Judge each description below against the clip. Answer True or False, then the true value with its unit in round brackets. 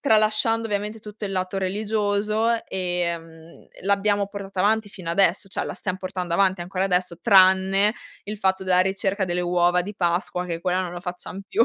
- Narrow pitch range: True (2.3 semitones)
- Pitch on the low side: False (190 Hz)